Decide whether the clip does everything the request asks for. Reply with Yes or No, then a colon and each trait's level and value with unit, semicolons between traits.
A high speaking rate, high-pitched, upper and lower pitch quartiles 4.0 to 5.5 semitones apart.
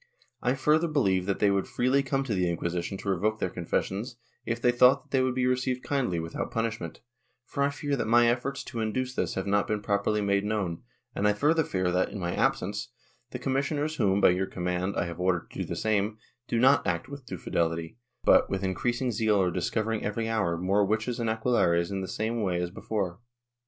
No: fast, 220 wpm; low, 105 Hz; average, 5.2 semitones